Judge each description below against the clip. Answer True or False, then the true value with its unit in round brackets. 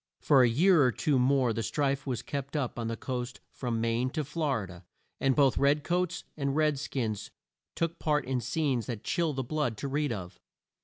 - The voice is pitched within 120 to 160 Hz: True (135 Hz)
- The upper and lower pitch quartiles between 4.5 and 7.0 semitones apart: False (3.7 semitones)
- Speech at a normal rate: False (210 wpm)